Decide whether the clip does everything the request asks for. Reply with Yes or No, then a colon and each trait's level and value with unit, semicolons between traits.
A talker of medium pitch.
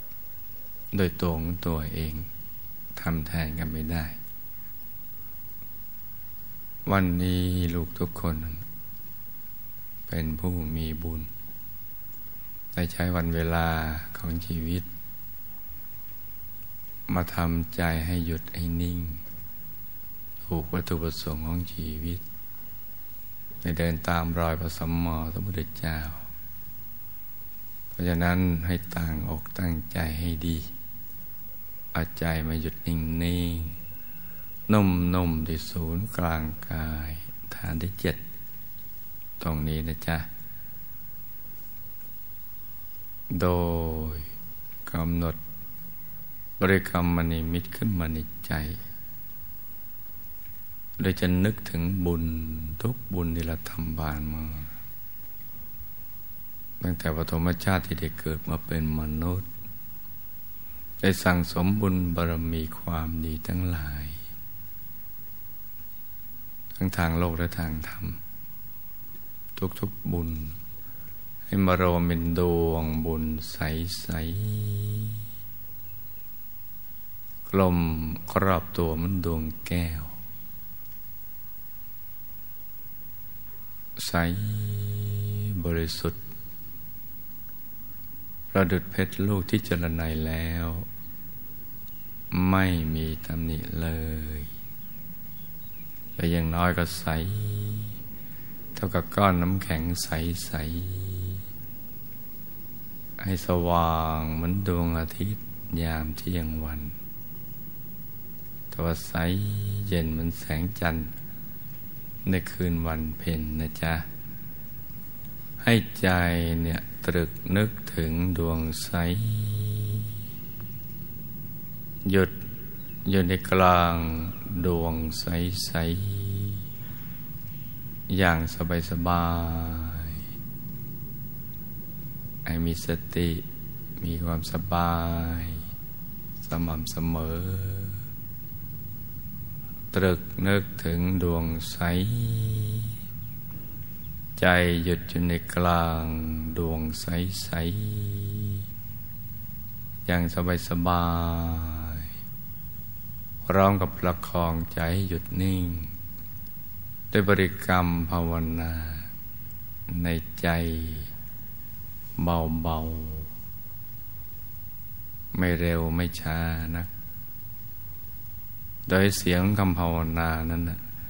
No: very low, 85 Hz